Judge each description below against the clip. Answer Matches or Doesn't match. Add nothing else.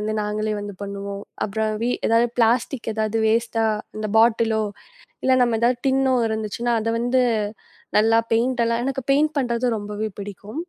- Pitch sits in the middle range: Doesn't match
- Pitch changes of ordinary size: Doesn't match